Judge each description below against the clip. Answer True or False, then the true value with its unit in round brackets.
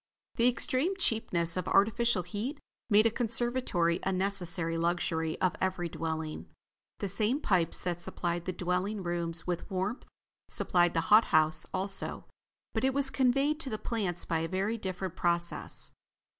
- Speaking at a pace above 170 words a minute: False (155 wpm)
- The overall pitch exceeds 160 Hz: True (185 Hz)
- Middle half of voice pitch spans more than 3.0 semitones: True (4.8 semitones)